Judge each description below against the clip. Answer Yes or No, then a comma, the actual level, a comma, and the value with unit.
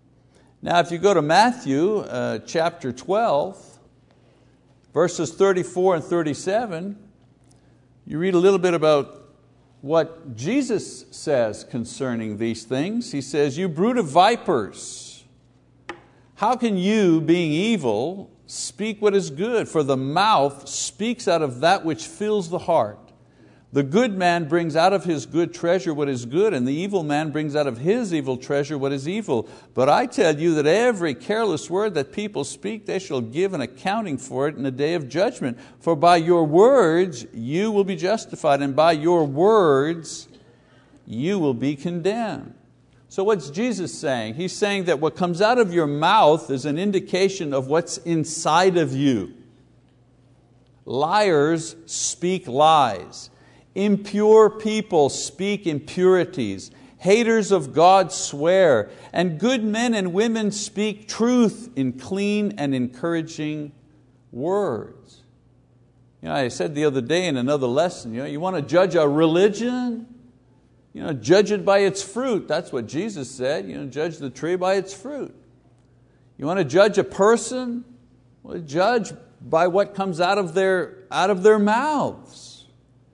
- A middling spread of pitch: No, wide, 5.9 semitones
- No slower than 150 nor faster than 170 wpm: Yes, average, 155 wpm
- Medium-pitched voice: Yes, medium, 170 Hz